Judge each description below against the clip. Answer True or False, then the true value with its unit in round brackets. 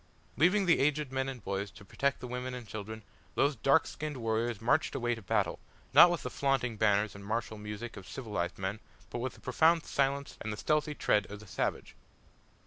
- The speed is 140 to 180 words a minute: False (205 wpm)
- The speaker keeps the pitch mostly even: False (4.8 semitones)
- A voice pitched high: False (120 Hz)